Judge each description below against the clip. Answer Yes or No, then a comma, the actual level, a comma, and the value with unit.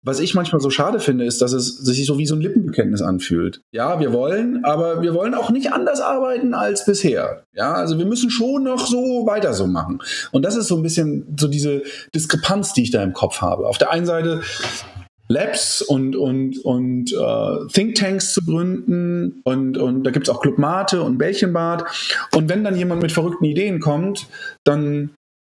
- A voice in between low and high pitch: Yes, medium, 165 Hz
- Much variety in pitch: Yes, wide, 7.1 semitones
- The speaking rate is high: Yes, fast, 200 wpm